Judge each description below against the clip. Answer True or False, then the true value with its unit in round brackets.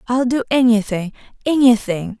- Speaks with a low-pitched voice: False (230 Hz)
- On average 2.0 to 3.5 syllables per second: False (4.8 syllables/s)